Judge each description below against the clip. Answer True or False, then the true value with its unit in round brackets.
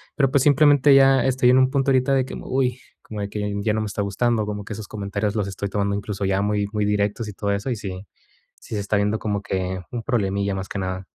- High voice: False (105 Hz)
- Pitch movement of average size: True (3.7 semitones)